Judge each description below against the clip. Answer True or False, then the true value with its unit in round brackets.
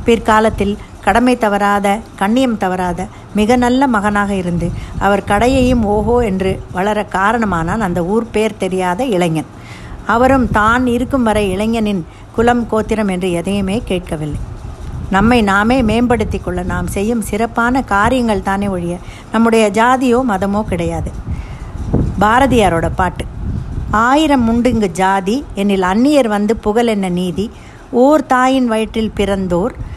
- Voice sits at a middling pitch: False (210 Hz)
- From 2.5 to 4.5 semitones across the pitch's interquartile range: True (3.8 semitones)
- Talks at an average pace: True (120 wpm)